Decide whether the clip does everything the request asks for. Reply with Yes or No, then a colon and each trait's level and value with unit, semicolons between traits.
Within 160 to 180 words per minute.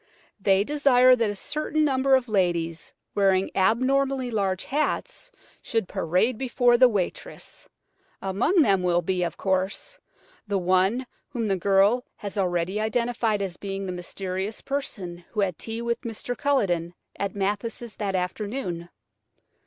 No: average, 140 wpm